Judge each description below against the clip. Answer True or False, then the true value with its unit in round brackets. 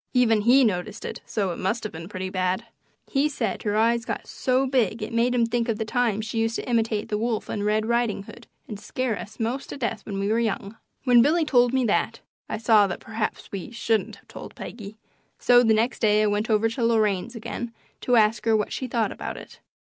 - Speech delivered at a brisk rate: True (235 wpm)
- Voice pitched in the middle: False (225 Hz)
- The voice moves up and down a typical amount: False (2.2 semitones)